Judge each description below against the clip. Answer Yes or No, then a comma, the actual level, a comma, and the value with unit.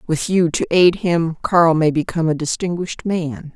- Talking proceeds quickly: No, average, 185 wpm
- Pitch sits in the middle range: Yes, medium, 165 Hz